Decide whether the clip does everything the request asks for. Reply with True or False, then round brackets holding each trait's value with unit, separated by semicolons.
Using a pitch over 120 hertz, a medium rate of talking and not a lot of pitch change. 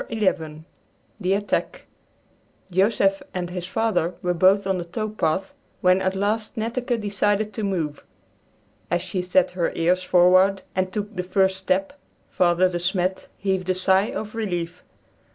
True (190 Hz; 150 wpm; 2.1 semitones)